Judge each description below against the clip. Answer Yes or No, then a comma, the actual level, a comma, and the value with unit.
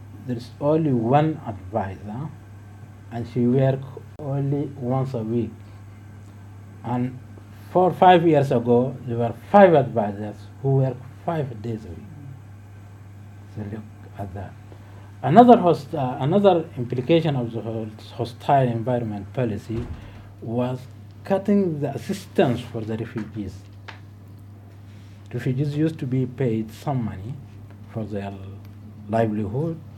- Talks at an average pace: No, slow, 115 wpm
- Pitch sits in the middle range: No, low, 115 Hz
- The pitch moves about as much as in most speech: Yes, average, 4.4 semitones